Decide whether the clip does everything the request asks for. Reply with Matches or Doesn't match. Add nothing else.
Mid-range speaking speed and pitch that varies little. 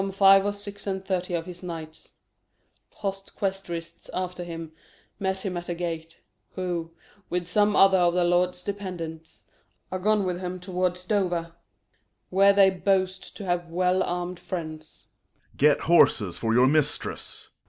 Matches